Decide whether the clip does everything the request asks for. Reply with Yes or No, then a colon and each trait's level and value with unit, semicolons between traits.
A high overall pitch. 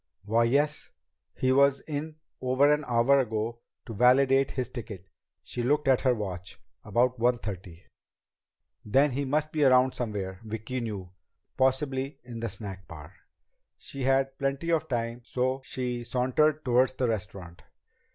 No: low, 125 Hz